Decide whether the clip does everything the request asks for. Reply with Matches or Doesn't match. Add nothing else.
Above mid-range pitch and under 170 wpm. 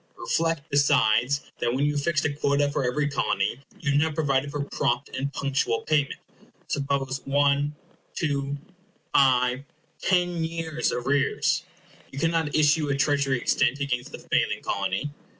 Doesn't match